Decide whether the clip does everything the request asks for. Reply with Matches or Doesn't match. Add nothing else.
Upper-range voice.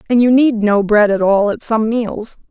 Matches